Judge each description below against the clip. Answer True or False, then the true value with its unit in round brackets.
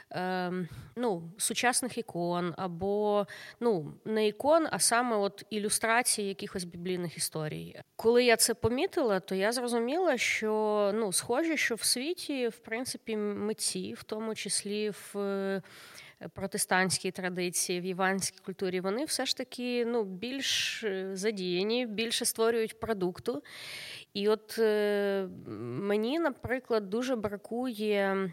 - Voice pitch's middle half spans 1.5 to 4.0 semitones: True (3.6 semitones)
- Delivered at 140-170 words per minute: False (115 wpm)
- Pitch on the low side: False (210 Hz)